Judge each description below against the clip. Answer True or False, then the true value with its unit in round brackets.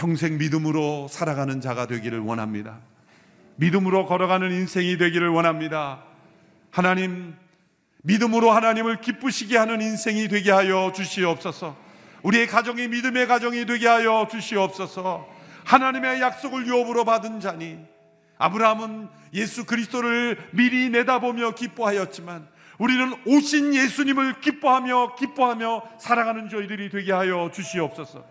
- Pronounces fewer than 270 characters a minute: False (340 characters per minute)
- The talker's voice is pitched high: True (205 Hz)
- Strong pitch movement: True (5.8 semitones)